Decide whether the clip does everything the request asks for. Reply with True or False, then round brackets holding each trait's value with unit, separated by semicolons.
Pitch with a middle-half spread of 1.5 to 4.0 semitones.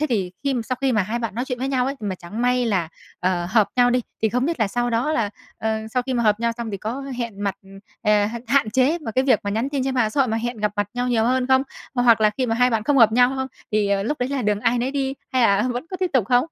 True (3.2 semitones)